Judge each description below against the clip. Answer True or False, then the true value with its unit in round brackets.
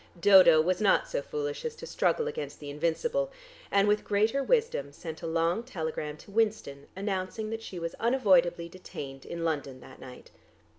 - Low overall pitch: False (190 Hz)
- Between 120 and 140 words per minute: False (175 wpm)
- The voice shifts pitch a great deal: True (6.4 semitones)